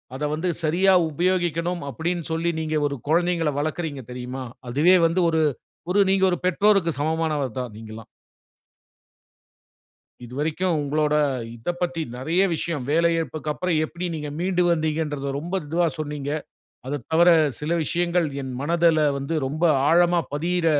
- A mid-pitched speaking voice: Yes, medium, 160 Hz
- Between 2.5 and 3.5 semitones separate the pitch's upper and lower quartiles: Yes, average, 3.0 semitones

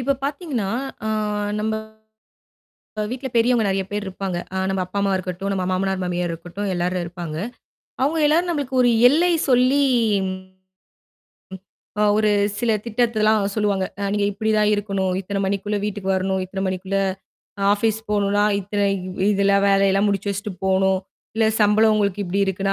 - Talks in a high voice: Yes, high, 200 Hz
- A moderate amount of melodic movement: No, narrow, 2.3 semitones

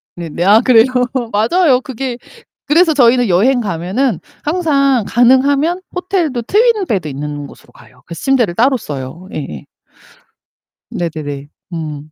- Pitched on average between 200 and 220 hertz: No, high, 235 Hz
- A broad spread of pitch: Yes, wide, 8.8 semitones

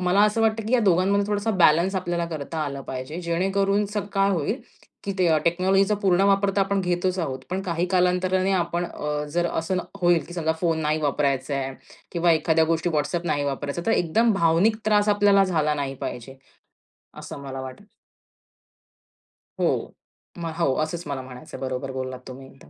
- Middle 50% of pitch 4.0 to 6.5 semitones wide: Yes, average, 4.4 semitones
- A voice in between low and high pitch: Yes, medium, 175 Hz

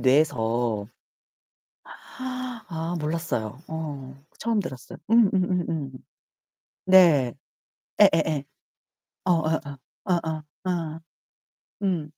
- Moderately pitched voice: Yes, medium, 160 Hz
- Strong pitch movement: No, average, 4.5 semitones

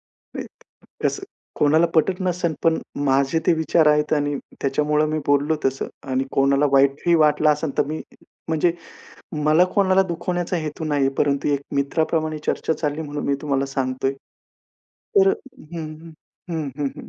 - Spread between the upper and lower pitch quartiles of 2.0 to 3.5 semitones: Yes, average, 2.7 semitones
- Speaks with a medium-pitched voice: Yes, medium, 150 Hz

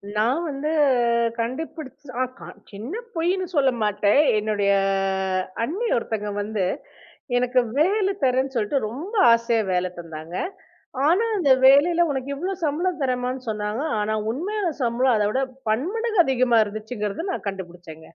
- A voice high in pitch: Yes, very high, 255 Hz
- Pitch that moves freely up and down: Yes, wide, 6.8 semitones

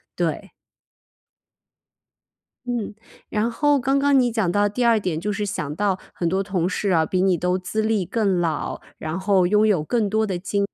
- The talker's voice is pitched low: No, high, 200 Hz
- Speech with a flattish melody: No, average, 3.3 semitones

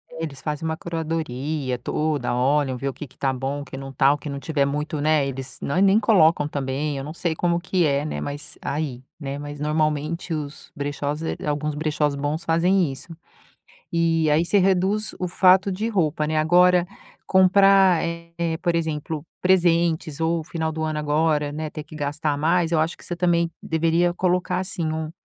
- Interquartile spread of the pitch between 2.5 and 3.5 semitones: Yes, average, 2.8 semitones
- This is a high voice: No, medium, 155 Hz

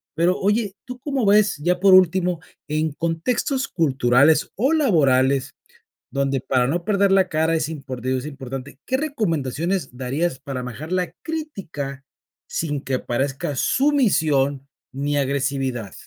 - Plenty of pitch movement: Yes, wide, 5.9 semitones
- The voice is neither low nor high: Yes, medium, 155 Hz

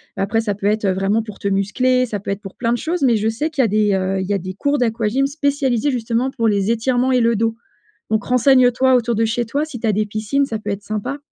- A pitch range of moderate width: Yes, average, 3.7 semitones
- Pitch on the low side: No, high, 225 Hz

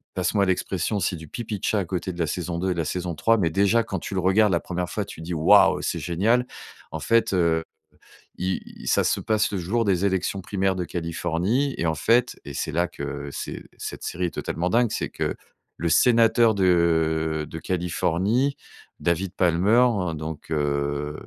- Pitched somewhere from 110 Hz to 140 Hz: No, very low, 90 Hz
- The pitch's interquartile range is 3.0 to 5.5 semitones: Yes, average, 3.8 semitones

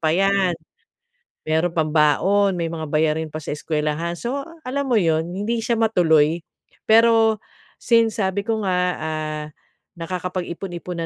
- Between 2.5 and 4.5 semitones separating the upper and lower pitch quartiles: No, wide, 5.5 semitones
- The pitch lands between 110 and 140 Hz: No, medium, 175 Hz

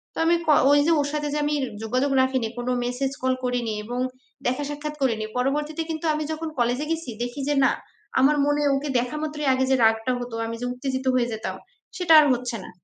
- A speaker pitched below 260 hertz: No, very high, 265 Hz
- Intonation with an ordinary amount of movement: Yes, average, 3.3 semitones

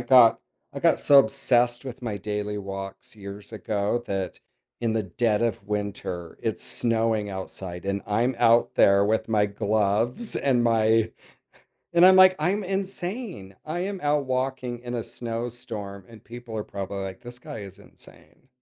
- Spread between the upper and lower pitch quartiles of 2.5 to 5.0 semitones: Yes, average, 3.6 semitones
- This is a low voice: Yes, low, 115 Hz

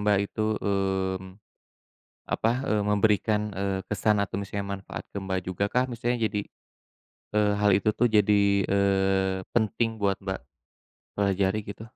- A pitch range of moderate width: No, narrow, 1.6 semitones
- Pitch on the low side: Yes, low, 100 Hz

